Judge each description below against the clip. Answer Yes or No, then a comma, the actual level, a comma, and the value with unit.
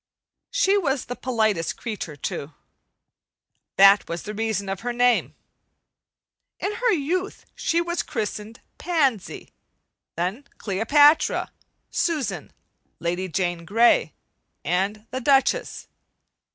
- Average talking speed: No, slow, 105 wpm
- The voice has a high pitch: Yes, high, 230 Hz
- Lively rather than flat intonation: Yes, wide, 7.1 semitones